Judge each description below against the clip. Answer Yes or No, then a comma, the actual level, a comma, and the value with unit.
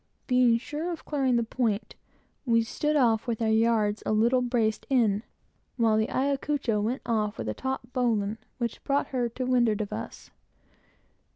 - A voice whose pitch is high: Yes, high, 235 Hz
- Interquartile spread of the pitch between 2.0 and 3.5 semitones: Yes, average, 2.9 semitones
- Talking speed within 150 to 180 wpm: Yes, average, 170 wpm